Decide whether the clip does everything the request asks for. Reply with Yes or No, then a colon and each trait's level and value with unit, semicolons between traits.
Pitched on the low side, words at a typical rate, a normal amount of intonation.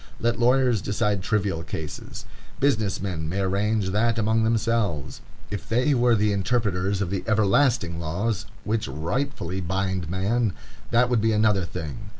Yes: low, 105 Hz; average, 150 wpm; average, 3.7 semitones